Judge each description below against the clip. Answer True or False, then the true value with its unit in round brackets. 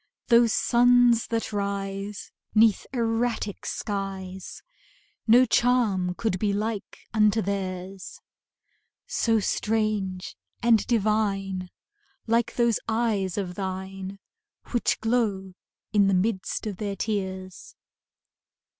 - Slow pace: True (100 wpm)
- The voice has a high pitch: True (205 Hz)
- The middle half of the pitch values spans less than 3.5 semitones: True (2.9 semitones)